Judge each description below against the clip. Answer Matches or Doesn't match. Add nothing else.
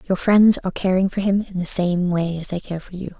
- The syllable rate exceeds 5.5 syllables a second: Matches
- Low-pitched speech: Doesn't match